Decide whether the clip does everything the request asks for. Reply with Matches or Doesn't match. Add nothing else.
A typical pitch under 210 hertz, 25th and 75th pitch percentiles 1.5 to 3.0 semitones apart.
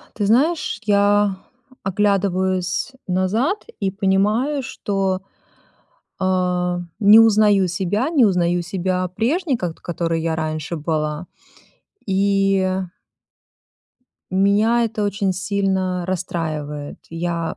Matches